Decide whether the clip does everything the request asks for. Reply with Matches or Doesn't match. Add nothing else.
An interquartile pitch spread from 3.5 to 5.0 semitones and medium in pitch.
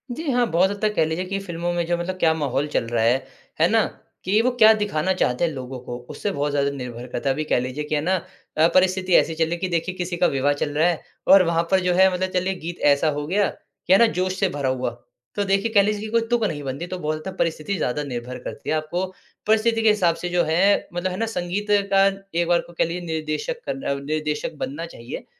Matches